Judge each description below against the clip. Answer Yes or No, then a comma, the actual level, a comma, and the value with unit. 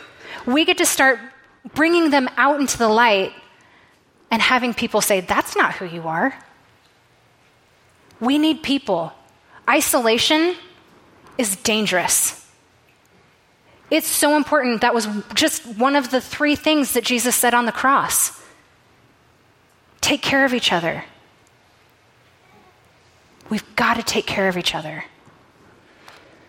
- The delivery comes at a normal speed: No, slow, 125 wpm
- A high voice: Yes, very high, 255 Hz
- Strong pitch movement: No, average, 4.7 semitones